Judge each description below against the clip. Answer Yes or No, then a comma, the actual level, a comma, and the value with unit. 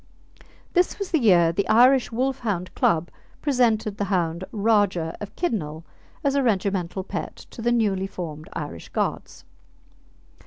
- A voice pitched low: No, high, 205 Hz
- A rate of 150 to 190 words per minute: No, average, 140 wpm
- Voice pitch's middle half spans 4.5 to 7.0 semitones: Yes, wide, 5.6 semitones